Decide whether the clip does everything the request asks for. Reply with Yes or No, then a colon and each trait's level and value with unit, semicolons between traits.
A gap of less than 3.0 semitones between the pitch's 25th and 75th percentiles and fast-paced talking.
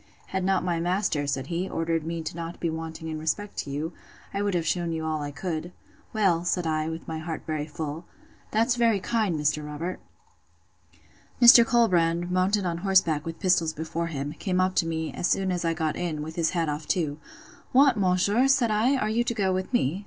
No: average, 3.3 semitones; fast, 210 wpm